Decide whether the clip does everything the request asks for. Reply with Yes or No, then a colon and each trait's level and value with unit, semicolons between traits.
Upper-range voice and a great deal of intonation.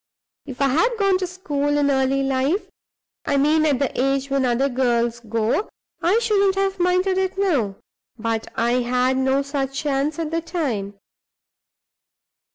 Yes: very high, 275 Hz; wide, 5.7 semitones